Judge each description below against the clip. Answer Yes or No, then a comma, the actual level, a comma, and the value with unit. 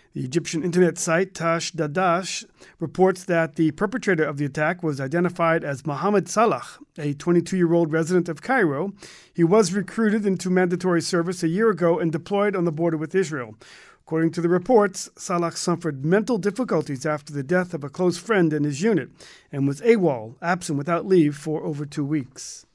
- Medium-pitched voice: Yes, medium, 170 Hz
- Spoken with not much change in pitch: No, average, 3.0 semitones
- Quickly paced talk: No, average, 180 wpm